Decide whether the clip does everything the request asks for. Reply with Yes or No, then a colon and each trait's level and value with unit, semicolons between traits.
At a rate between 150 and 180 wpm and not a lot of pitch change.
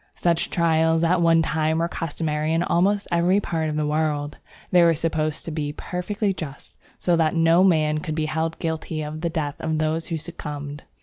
No: average, 195 wpm; narrow, 1.7 semitones